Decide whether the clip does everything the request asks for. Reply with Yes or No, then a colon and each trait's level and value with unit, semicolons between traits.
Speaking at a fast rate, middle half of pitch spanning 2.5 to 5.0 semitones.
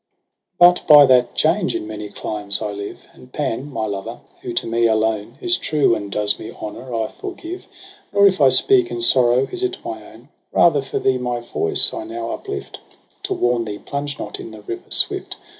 No: fast, 210 wpm; wide, 5.5 semitones